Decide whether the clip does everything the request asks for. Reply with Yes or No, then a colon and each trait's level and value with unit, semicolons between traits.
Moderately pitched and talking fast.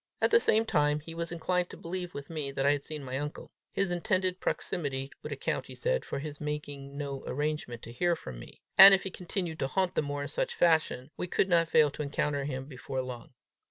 Yes: medium, 150 Hz; fast, 230 wpm